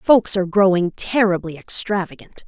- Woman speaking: Yes, female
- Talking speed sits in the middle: No, slow, 120 wpm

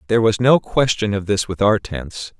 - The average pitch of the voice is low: Yes, low, 105 Hz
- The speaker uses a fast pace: Yes, fast, 225 wpm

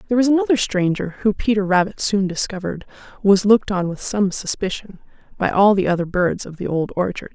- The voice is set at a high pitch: Yes, high, 200 Hz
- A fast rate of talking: No, average, 195 wpm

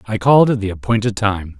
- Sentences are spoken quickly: Yes, fast, 225 wpm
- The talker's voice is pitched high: No, low, 110 Hz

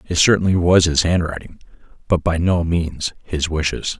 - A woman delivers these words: No, male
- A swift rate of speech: No, average, 165 wpm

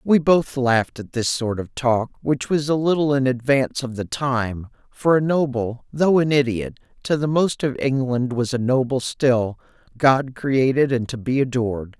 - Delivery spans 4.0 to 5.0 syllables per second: Yes, 4.5 syllables/s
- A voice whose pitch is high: No, low, 130 Hz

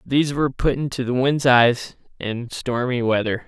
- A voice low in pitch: Yes, low, 125 Hz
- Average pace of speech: Yes, average, 175 wpm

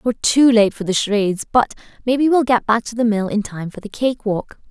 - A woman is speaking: Yes, female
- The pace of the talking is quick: Yes, fast, 255 wpm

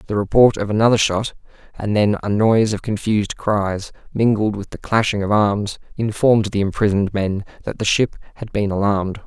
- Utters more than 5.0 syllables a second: Yes, 5.5 syllables/s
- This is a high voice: No, low, 105 Hz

